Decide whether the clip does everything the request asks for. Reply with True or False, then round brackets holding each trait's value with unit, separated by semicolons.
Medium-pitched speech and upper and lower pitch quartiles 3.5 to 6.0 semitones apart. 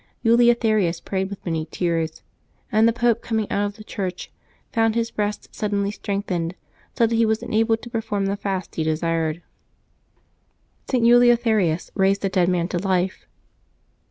False (200 Hz; 4.1 semitones)